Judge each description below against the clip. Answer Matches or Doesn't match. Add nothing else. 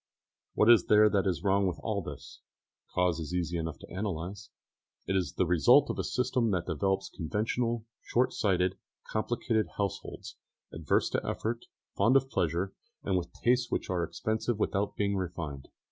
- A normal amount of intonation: Matches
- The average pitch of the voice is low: Matches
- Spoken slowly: Doesn't match